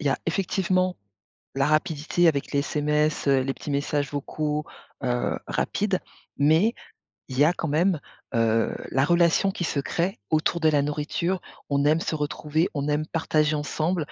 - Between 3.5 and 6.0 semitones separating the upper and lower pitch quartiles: No, average, 2.9 semitones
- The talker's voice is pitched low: No, medium, 150 Hz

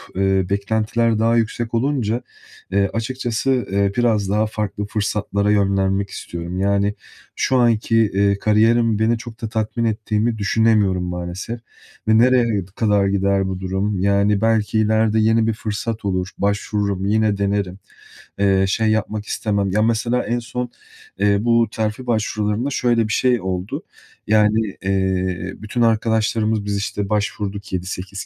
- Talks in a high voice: No, low, 105 Hz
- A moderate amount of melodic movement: No, narrow, 2.2 semitones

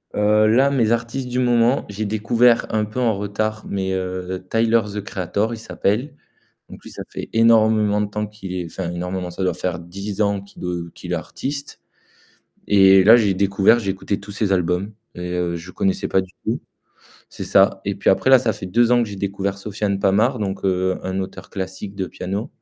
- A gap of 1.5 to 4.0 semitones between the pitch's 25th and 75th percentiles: Yes, average, 2.8 semitones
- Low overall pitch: Yes, low, 100 Hz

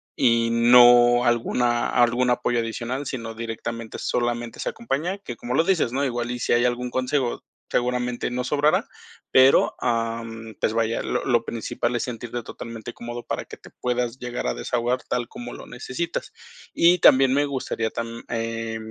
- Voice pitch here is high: No, low, 120 Hz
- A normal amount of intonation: No, narrow, 1.5 semitones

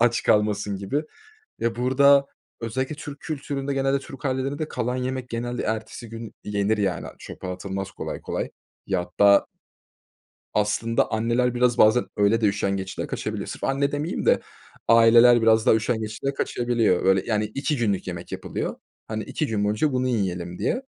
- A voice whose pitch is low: Yes, low, 115 Hz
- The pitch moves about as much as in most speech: Yes, average, 4.0 semitones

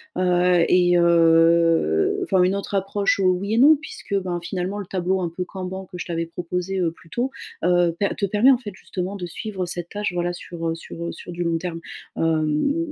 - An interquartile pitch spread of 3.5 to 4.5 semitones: No, narrow, 2.6 semitones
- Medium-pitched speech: Yes, medium, 180 Hz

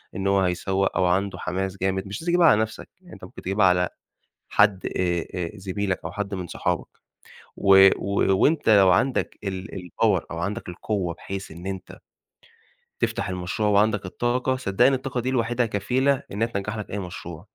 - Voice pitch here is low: Yes, low, 100 Hz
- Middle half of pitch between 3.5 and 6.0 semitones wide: No, average, 3.1 semitones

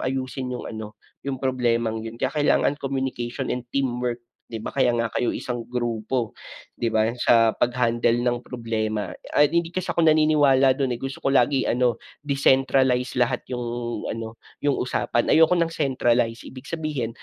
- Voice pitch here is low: Yes, low, 125 Hz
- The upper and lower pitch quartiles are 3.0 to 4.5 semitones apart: No, narrow, 2.6 semitones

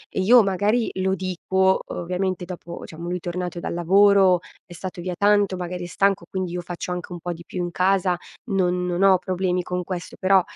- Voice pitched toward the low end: No, medium, 180 Hz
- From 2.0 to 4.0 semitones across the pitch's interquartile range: No, narrow, 1.3 semitones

